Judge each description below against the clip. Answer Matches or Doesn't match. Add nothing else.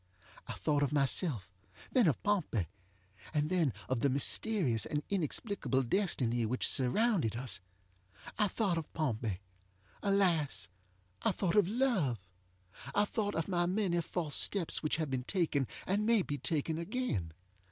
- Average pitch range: Doesn't match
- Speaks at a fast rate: Doesn't match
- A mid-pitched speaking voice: Matches